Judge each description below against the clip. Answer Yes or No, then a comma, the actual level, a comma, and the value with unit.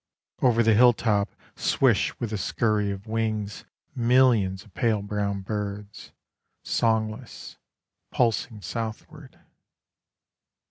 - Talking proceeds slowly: Yes, slow, 95 wpm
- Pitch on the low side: Yes, low, 110 Hz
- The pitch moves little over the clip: Yes, narrow, 2.3 semitones